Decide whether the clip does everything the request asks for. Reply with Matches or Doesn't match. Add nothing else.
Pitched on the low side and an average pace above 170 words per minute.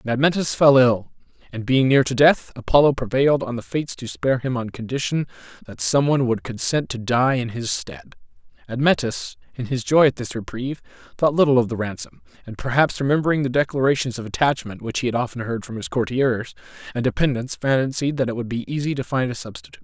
Matches